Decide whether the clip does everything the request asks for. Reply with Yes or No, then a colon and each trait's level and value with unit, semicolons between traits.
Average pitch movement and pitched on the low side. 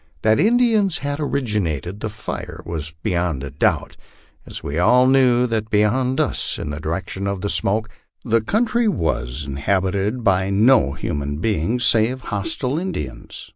No: wide, 6.9 semitones; low, 105 Hz